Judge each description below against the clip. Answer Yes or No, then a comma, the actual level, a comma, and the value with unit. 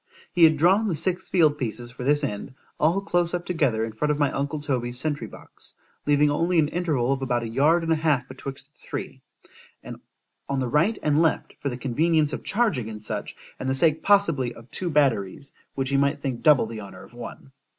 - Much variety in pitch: No, average, 4.4 semitones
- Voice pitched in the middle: Yes, medium, 145 Hz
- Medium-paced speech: No, fast, 210 wpm